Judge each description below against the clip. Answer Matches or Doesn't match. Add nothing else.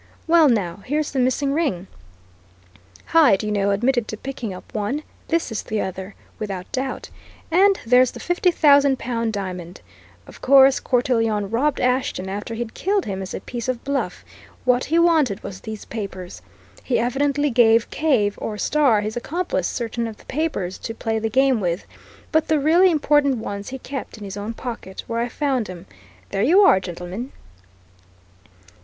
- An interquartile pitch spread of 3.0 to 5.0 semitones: Doesn't match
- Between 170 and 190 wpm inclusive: Matches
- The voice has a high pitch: Matches